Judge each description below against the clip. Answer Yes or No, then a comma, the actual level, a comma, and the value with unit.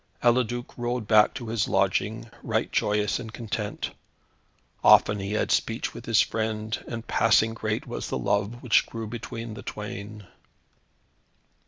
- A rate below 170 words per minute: Yes, average, 145 wpm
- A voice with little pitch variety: Yes, narrow, 1.9 semitones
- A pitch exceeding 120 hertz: No, low, 110 Hz